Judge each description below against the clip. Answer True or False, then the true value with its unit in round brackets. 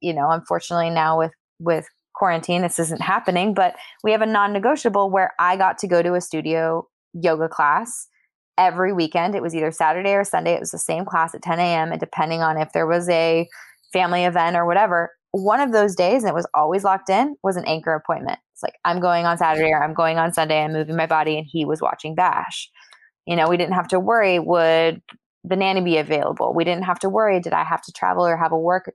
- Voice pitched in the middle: True (170 Hz)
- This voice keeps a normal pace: False (235 wpm)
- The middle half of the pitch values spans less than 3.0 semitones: True (2.5 semitones)